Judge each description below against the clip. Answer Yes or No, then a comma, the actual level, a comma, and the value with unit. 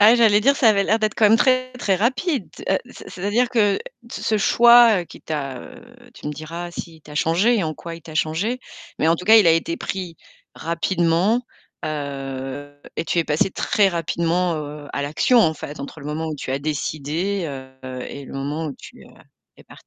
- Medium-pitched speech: Yes, medium, 170 Hz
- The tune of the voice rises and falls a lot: Yes, wide, 5.9 semitones